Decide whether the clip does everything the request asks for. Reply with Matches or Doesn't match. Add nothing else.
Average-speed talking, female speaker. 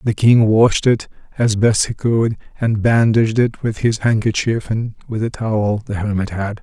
Doesn't match